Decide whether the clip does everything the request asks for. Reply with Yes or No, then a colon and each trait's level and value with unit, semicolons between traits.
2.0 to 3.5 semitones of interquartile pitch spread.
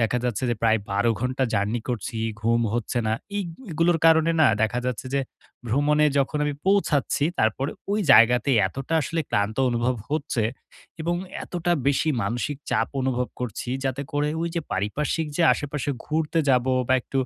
No: average, 4.4 semitones